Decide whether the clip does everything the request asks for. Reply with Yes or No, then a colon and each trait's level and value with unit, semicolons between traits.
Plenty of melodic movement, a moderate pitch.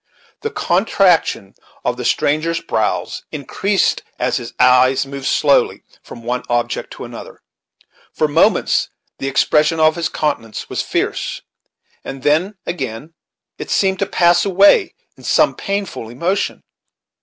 Yes: wide, 6.0 semitones; medium, 150 Hz